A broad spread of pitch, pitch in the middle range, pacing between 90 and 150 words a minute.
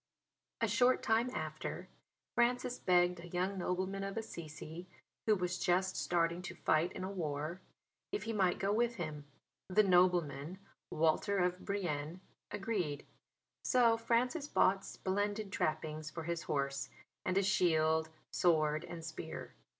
No: average, 4.1 semitones; medium, 180 Hz; average, 140 wpm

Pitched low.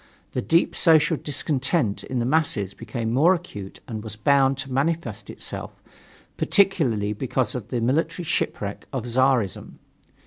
Yes: low, 130 Hz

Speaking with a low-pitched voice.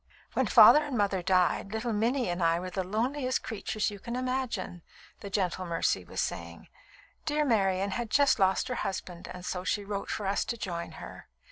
No: high, 200 Hz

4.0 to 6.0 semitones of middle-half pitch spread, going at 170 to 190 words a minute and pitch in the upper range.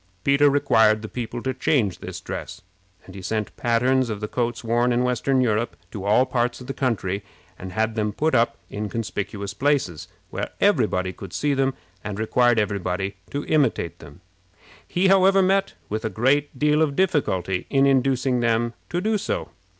No: average, 4.6 semitones; average, 185 wpm; low, 120 Hz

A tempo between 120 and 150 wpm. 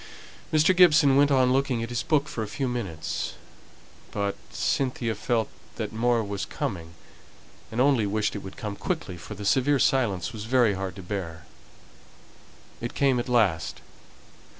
No: average, 160 wpm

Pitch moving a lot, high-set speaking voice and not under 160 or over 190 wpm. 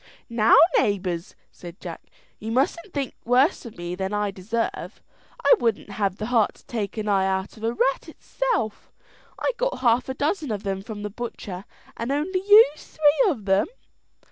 Yes: wide, 5.9 semitones; high, 225 Hz; average, 180 wpm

